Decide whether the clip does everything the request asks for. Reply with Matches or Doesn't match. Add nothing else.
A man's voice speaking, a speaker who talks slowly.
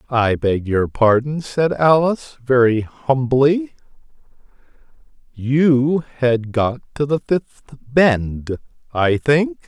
Matches